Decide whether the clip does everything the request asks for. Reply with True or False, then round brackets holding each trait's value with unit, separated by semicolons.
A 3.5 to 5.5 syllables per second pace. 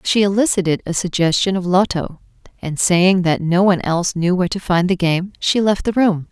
True (5.4 syllables/s)